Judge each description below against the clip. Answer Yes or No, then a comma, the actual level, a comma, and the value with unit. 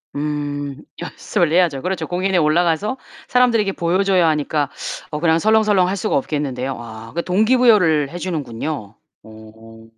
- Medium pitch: Yes, medium, 160 Hz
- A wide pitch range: No, average, 4.8 semitones